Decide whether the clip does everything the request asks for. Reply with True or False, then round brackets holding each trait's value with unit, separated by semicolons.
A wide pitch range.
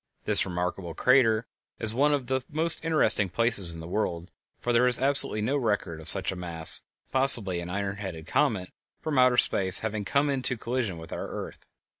True (6.1 semitones)